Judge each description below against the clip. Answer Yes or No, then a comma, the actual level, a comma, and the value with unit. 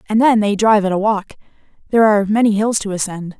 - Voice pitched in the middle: No, high, 210 Hz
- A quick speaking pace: Yes, fast, 230 wpm